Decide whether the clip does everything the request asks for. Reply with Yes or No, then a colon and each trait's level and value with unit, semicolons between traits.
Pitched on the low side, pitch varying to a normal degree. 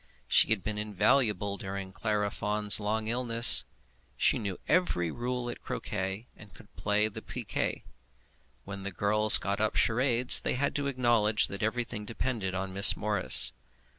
Yes: low, 105 Hz; average, 3.0 semitones